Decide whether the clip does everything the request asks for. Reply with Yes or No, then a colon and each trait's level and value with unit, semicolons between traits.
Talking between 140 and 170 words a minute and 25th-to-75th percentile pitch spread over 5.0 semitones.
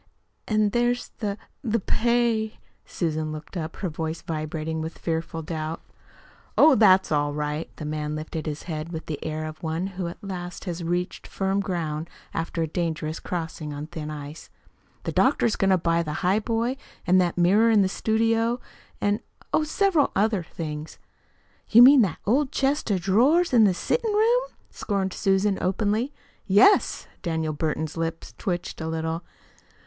Yes: average, 165 wpm; wide, 5.4 semitones